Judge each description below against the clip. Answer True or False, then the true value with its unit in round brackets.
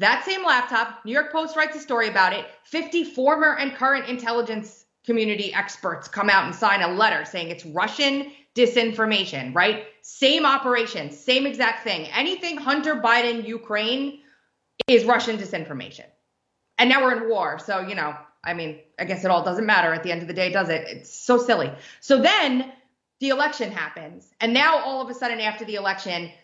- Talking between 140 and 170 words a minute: False (185 wpm)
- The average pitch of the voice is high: True (230 Hz)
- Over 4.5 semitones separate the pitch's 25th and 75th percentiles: True (5.6 semitones)